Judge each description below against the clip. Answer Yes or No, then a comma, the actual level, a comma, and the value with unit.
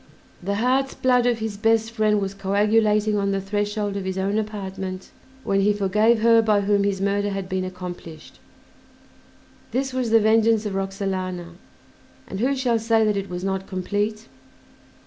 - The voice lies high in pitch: Yes, high, 205 Hz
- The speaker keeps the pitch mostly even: Yes, narrow, 2.3 semitones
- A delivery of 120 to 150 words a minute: No, average, 165 wpm